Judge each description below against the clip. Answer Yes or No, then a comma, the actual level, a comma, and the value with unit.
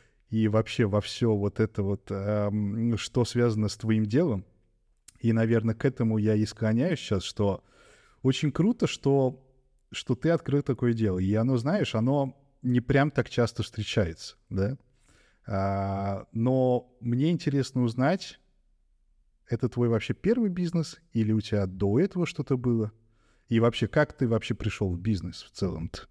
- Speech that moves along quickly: No, average, 150 wpm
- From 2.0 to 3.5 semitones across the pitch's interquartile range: No, average, 4.0 semitones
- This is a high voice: No, low, 115 Hz